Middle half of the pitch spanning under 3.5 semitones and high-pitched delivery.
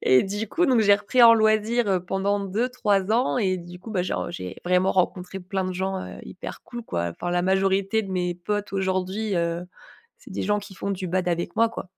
Yes: average, 2.8 semitones; high, 195 Hz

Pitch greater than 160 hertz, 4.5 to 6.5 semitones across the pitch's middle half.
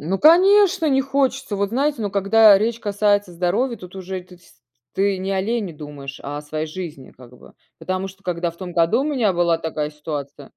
Yes: high, 190 Hz; wide, 5.4 semitones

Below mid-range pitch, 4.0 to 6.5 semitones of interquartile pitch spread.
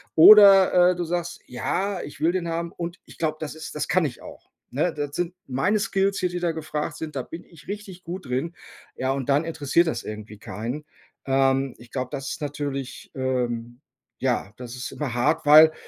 No: medium, 155 Hz; average, 4.8 semitones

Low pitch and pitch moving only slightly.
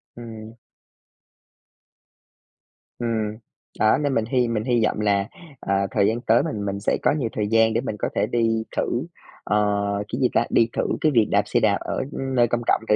Yes: low, 110 Hz; narrow, 2.2 semitones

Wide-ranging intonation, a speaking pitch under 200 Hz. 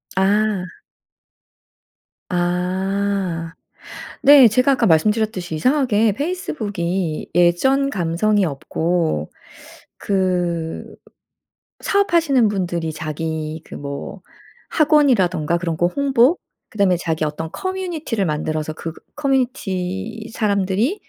Yes: wide, 6.5 semitones; high, 190 Hz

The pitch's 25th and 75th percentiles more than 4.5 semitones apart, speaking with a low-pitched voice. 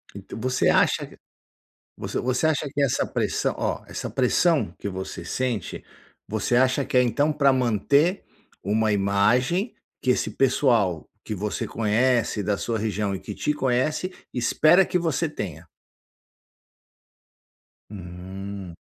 Yes: wide, 5.5 semitones; low, 120 Hz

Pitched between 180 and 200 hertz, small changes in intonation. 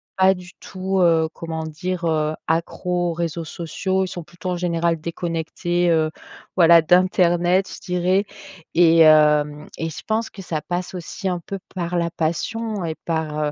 No: medium, 170 Hz; narrow, 2.1 semitones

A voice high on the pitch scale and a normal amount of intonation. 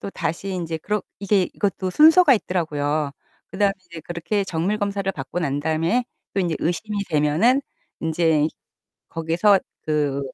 No: medium, 175 Hz; average, 4.2 semitones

